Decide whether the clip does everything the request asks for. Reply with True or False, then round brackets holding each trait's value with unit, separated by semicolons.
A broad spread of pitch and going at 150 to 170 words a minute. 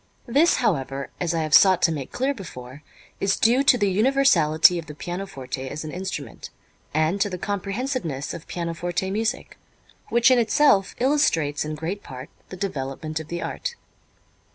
True (6.3 semitones; 165 wpm)